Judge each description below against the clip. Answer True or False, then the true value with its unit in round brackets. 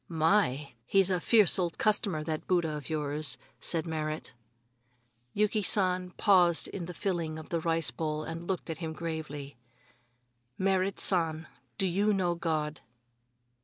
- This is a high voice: False (165 Hz)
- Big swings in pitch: False (3.1 semitones)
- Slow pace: False (145 wpm)